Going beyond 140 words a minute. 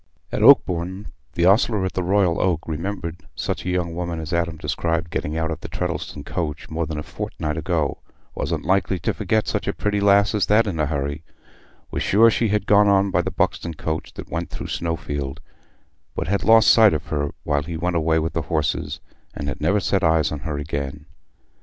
Yes: fast, 205 wpm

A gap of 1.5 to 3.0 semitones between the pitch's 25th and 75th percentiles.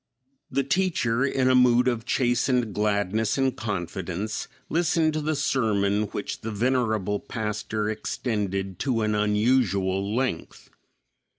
No: average, 4.0 semitones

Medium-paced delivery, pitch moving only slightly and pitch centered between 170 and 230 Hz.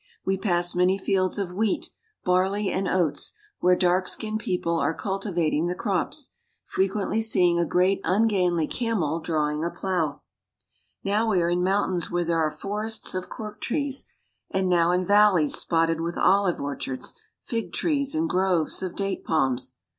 No: average, 165 wpm; average, 3.0 semitones; medium, 185 Hz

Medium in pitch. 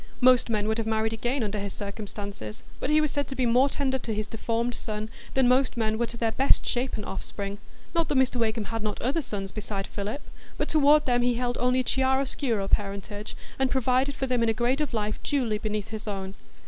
No: high, 230 Hz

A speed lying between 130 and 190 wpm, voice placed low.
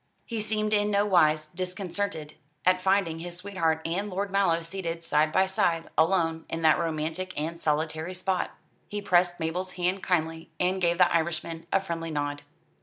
No: average, 170 wpm; medium, 175 Hz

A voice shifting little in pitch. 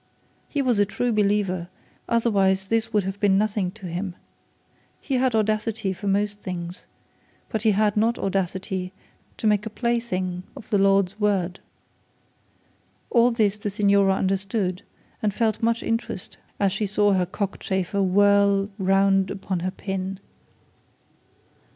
Yes: narrow, 2.1 semitones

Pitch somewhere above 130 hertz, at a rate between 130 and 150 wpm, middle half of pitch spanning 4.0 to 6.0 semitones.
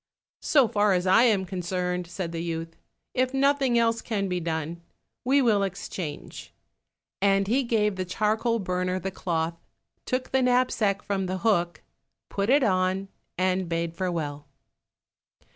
Yes: high, 190 Hz; average, 145 wpm; average, 4.5 semitones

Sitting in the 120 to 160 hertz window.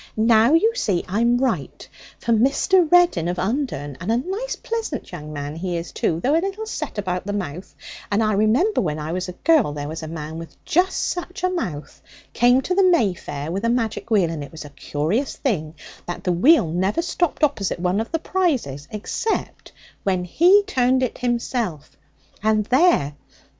No: high, 215 Hz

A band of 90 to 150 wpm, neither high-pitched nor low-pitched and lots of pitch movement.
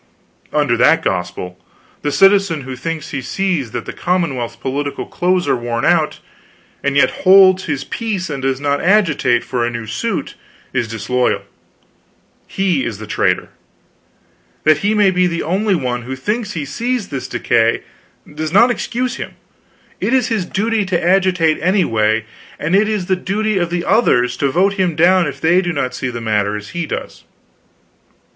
No: average, 175 wpm; medium, 160 Hz; wide, 7.0 semitones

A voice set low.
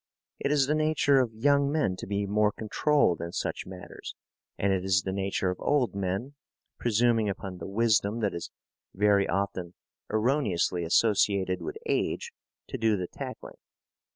Yes: low, 105 Hz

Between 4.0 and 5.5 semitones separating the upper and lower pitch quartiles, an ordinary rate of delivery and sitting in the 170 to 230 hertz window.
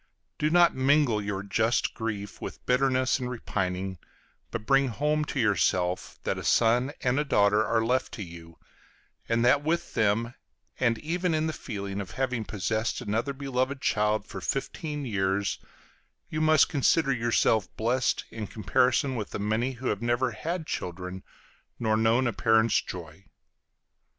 No: average, 4.4 semitones; average, 155 wpm; low, 115 Hz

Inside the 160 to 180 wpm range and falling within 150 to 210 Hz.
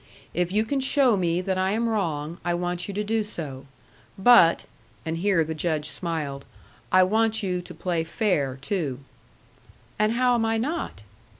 Yes: average, 175 wpm; medium, 185 Hz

